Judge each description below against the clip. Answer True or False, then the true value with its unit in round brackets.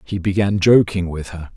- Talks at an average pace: True (190 wpm)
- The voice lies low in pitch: True (95 Hz)